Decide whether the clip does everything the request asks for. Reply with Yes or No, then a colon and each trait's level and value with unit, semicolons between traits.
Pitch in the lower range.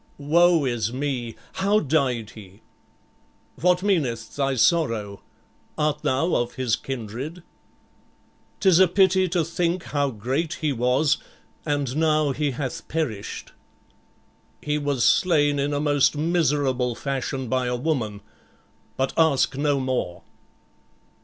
No: medium, 145 Hz